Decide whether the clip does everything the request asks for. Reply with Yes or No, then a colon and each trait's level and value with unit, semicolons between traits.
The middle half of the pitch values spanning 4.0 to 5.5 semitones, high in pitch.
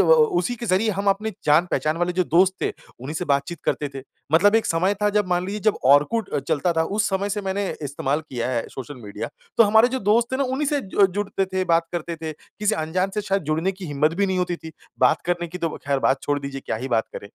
No: average, 5.1 semitones; medium, 180 Hz